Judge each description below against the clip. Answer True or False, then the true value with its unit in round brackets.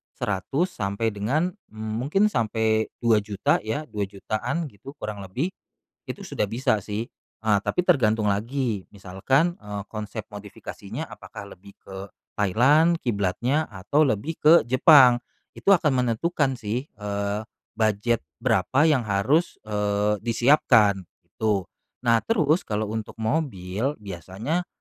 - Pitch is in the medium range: False (110 Hz)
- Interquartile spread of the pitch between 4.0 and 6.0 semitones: True (5.1 semitones)